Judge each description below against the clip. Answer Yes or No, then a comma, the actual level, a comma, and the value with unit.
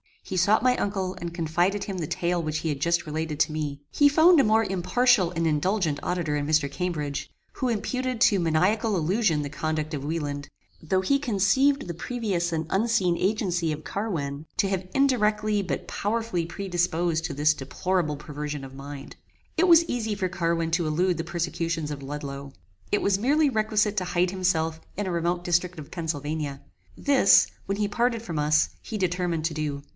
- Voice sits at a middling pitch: Yes, medium, 175 Hz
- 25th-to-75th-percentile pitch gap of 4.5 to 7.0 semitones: Yes, average, 4.9 semitones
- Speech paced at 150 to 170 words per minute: No, average, 185 wpm